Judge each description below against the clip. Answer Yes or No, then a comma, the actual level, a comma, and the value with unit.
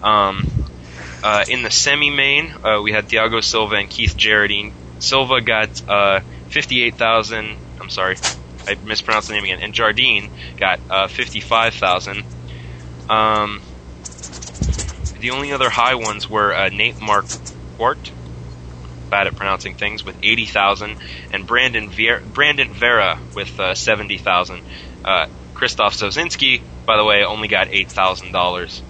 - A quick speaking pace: No, slow, 135 wpm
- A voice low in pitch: Yes, very low, 90 Hz